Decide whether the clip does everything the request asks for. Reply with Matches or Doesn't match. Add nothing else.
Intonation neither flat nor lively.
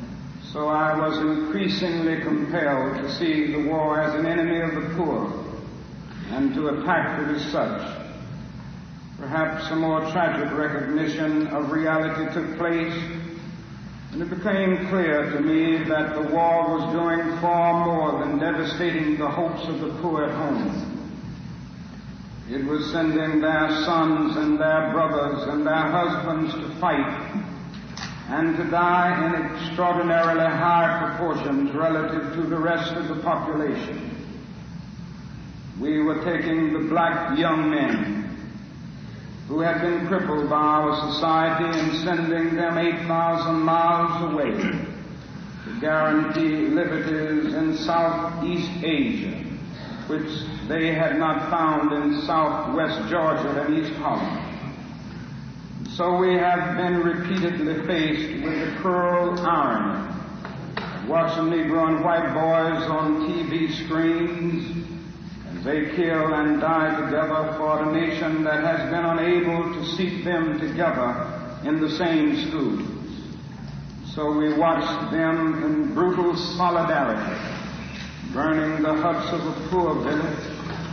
Doesn't match